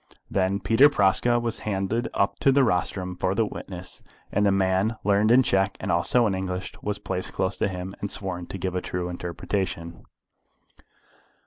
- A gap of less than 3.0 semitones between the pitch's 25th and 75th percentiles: Yes, narrow, 2.4 semitones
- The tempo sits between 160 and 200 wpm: Yes, average, 180 wpm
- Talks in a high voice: No, very low, 95 Hz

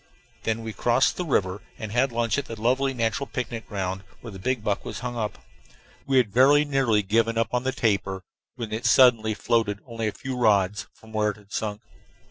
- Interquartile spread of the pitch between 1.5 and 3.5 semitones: Yes, average, 3.0 semitones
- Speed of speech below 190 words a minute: No, average, 200 wpm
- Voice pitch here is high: No, low, 115 Hz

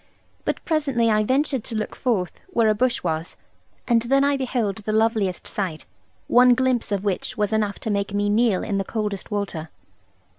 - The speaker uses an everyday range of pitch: Yes, average, 3.5 semitones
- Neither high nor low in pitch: No, high, 215 Hz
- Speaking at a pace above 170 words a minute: Yes, average, 185 wpm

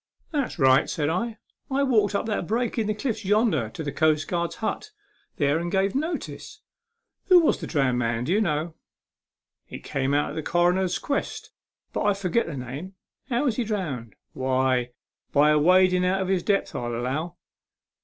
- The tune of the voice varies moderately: No, wide, 6.7 semitones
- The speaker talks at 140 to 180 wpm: No, average, 195 wpm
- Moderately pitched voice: Yes, medium, 175 Hz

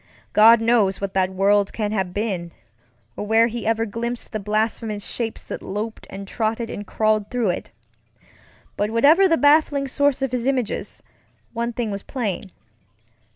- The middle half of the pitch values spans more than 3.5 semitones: No, average, 2.7 semitones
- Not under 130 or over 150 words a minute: No, average, 160 wpm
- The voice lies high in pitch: Yes, high, 225 Hz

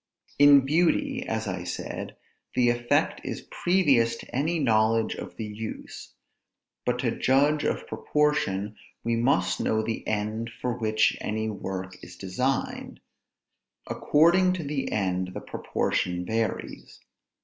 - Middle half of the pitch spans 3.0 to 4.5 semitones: No, average, 5.1 semitones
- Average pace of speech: No, slow, 130 wpm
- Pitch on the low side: Yes, low, 115 Hz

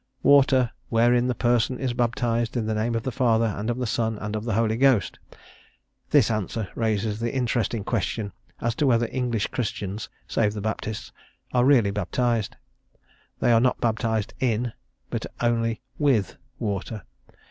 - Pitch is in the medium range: No, low, 115 Hz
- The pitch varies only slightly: Yes, narrow, 2.0 semitones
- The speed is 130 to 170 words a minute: Yes, average, 160 wpm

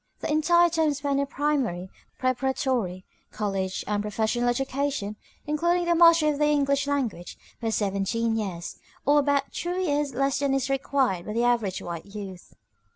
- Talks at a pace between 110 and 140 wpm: No, average, 155 wpm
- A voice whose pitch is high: Yes, very high, 265 Hz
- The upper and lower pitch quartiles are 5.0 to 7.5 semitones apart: Yes, wide, 5.6 semitones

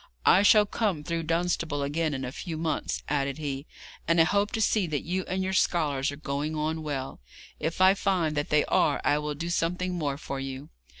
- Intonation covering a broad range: No, average, 3.5 semitones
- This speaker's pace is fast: Yes, fast, 215 wpm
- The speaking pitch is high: No, medium, 155 Hz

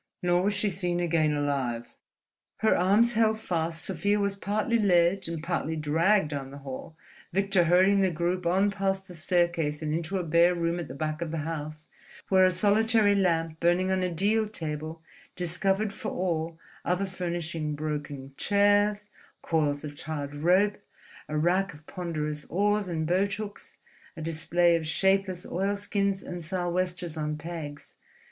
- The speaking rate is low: No, average, 160 wpm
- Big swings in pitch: No, average, 3.7 semitones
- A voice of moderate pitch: Yes, medium, 175 Hz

